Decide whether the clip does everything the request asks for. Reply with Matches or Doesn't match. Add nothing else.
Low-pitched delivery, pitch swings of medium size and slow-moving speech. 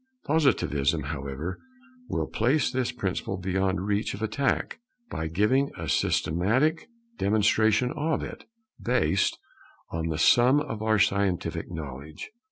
Doesn't match